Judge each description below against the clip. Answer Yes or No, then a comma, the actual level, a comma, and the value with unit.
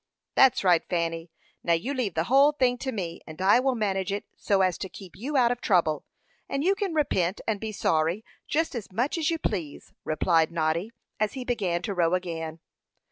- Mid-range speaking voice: No, high, 195 Hz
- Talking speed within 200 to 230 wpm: Yes, fast, 205 wpm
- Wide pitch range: Yes, wide, 6.8 semitones